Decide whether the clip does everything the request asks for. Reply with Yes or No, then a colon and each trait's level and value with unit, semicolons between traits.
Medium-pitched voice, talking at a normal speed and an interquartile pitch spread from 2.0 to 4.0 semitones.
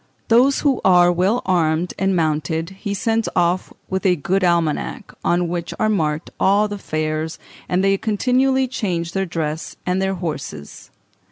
Yes: medium, 180 Hz; average, 160 wpm; average, 3.6 semitones